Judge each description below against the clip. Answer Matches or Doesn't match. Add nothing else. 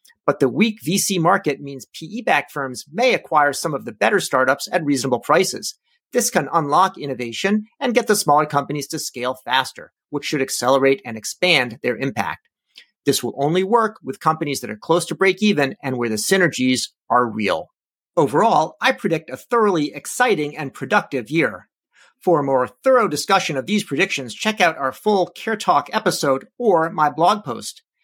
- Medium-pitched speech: Matches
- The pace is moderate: Matches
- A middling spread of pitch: Doesn't match